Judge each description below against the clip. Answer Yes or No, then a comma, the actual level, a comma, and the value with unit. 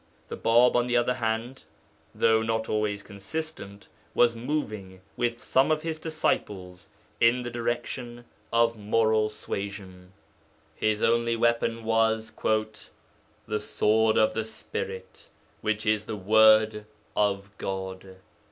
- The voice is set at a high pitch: No, low, 110 Hz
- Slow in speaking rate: Yes, slow, 125 wpm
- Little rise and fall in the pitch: Yes, narrow, 2.2 semitones